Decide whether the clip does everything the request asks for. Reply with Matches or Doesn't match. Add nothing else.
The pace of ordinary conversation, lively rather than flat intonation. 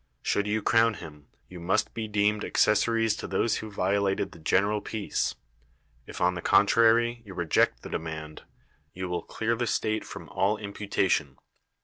Doesn't match